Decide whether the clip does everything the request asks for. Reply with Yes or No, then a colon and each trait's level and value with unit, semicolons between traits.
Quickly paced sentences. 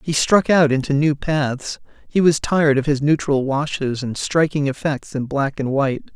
No: average, 195 wpm